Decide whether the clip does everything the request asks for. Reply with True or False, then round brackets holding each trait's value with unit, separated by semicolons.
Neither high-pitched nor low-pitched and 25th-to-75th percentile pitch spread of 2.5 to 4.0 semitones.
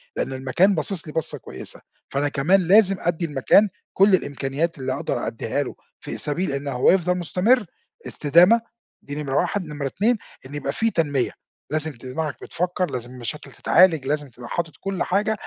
False (155 Hz; 5.0 semitones)